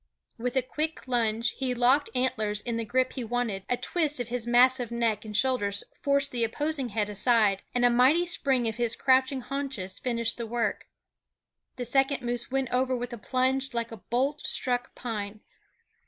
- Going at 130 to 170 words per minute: No, average, 185 wpm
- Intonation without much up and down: Yes, narrow, 2.3 semitones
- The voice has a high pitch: Yes, high, 245 Hz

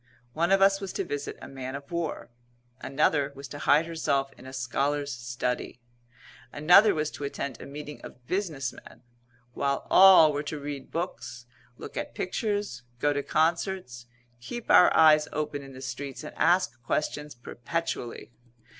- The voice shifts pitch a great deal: No, average, 4.0 semitones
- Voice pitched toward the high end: No, medium, 145 Hz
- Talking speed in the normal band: Yes, average, 165 wpm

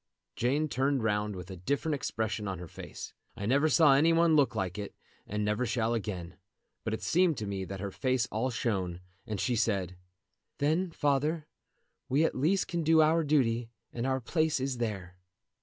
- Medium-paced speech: Yes, average, 190 wpm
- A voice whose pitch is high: No, low, 120 Hz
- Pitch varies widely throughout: Yes, wide, 6.3 semitones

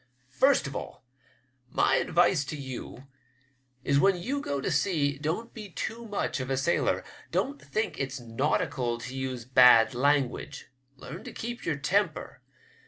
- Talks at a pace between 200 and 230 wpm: No, average, 155 wpm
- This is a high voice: No, medium, 140 Hz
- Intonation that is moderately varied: No, wide, 6.8 semitones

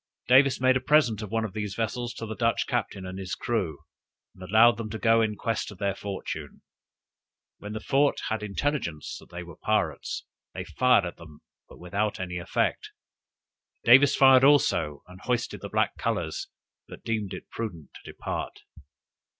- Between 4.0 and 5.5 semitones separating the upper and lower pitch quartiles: Yes, average, 4.7 semitones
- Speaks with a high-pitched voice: No, low, 110 Hz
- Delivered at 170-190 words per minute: Yes, average, 175 wpm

